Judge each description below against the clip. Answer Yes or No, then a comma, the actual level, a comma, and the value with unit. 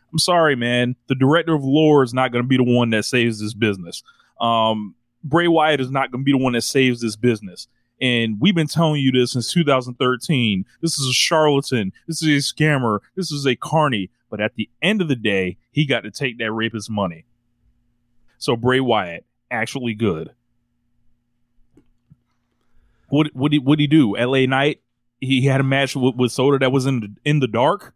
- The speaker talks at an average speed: Yes, average, 195 wpm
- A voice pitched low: Yes, low, 125 Hz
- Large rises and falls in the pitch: No, average, 3.4 semitones